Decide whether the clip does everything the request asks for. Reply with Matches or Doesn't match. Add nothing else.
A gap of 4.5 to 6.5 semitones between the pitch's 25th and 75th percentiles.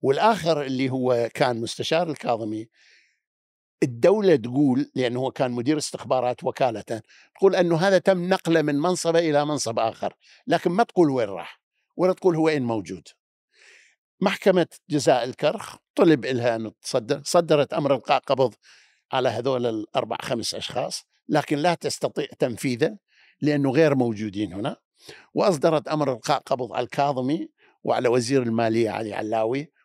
Matches